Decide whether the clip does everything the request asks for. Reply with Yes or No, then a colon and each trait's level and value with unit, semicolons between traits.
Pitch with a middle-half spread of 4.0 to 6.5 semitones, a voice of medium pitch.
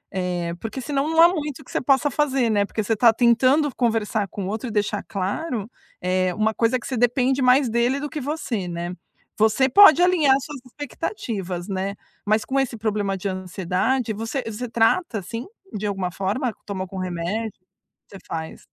No: average, 5.2 semitones; high, 225 Hz